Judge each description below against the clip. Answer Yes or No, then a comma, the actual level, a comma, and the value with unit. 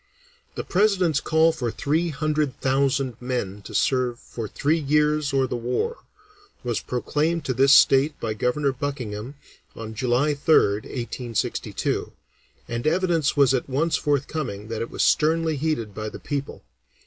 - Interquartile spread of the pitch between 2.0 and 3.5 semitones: No, average, 4.1 semitones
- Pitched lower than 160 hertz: Yes, low, 135 Hz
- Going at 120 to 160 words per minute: Yes, average, 150 wpm